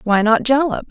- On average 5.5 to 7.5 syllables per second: No, 5.1 syllables/s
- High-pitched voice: Yes, high, 235 Hz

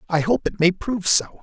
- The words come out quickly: Yes, fast, 250 wpm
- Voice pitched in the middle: Yes, medium, 180 Hz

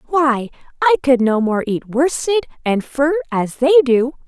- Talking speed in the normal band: Yes, average, 170 wpm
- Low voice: No, very high, 275 Hz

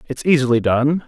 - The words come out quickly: No, average, 165 wpm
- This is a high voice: No, low, 135 Hz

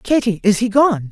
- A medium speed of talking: No, fast, 215 wpm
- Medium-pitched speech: No, high, 225 Hz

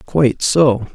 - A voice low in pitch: Yes, low, 130 Hz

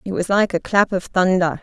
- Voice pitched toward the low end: No, medium, 185 Hz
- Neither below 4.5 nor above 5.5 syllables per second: Yes, 5.2 syllables/s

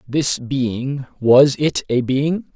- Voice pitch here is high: No, low, 135 Hz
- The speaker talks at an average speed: No, slow, 115 wpm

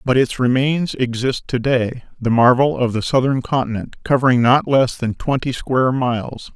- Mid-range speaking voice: No, low, 125 Hz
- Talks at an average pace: Yes, average, 175 wpm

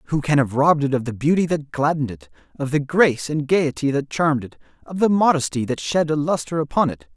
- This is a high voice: No, medium, 145 Hz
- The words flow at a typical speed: No, fast, 235 wpm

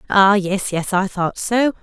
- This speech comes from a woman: Yes, female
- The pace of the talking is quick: No, average, 195 wpm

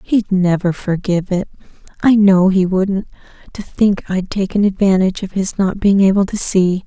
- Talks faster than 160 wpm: No, average, 155 wpm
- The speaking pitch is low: No, high, 190 Hz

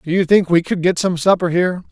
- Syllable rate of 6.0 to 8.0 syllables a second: Yes, 6.3 syllables/s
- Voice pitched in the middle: Yes, medium, 180 Hz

